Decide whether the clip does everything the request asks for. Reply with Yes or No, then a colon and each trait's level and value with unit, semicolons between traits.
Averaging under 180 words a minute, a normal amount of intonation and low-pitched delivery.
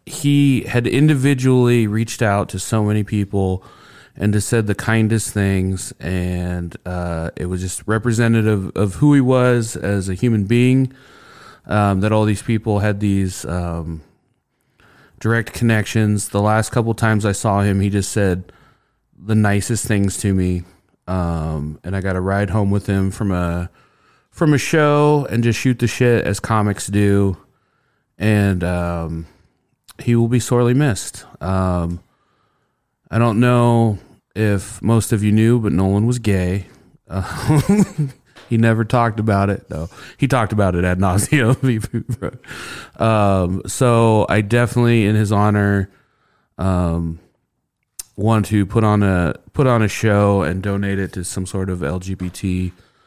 Yes: average, 155 wpm; average, 3.7 semitones; low, 105 Hz